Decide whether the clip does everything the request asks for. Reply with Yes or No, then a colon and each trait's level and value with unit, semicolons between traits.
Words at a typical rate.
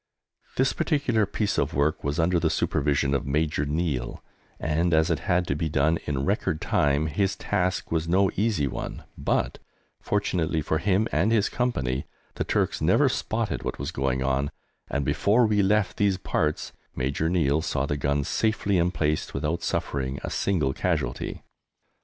Yes: average, 165 wpm